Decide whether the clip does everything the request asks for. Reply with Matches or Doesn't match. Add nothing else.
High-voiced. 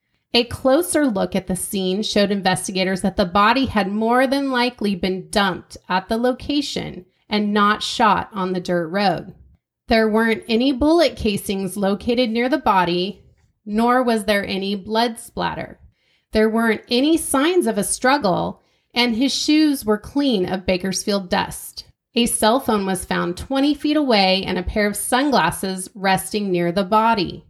Matches